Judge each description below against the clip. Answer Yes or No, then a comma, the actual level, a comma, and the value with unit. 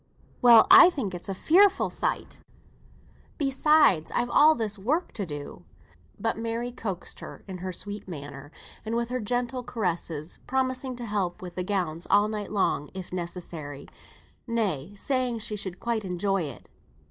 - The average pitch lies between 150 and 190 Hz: No, high, 205 Hz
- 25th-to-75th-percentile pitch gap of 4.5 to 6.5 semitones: Yes, average, 5.3 semitones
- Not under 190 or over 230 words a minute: No, average, 155 wpm